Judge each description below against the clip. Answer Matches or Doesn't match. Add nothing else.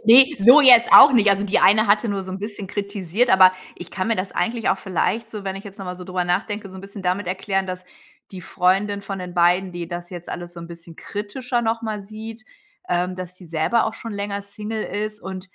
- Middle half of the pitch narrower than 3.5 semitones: Matches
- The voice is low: Doesn't match